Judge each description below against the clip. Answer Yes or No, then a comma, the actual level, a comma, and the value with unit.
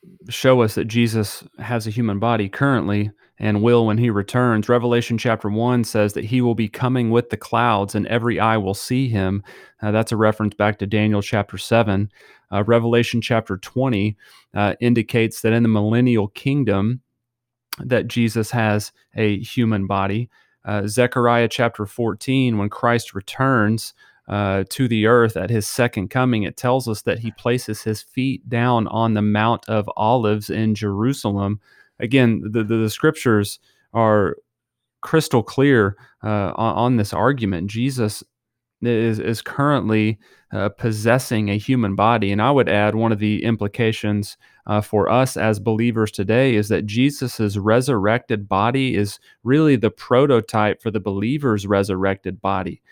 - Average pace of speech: Yes, average, 160 wpm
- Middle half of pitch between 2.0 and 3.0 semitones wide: Yes, narrow, 2.4 semitones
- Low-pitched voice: Yes, low, 110 Hz